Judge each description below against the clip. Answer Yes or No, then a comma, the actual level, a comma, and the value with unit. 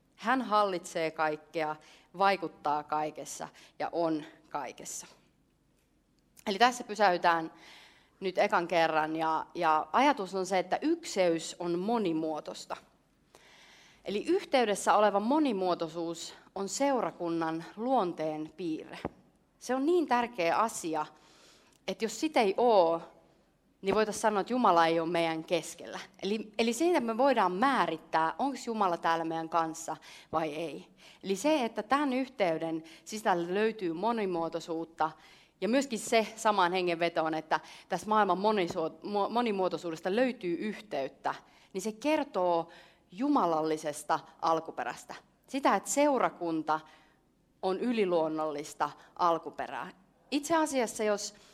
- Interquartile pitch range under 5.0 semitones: No, wide, 5.4 semitones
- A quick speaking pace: No, average, 115 wpm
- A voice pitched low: No, medium, 180 Hz